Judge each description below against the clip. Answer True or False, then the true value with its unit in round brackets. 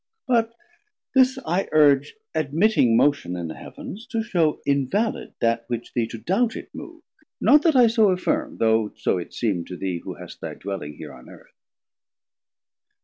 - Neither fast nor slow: True (170 wpm)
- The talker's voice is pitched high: False (150 Hz)